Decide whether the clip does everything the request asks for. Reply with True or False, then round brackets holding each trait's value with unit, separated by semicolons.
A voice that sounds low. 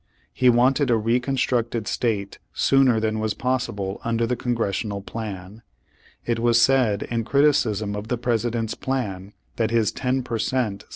True (115 Hz)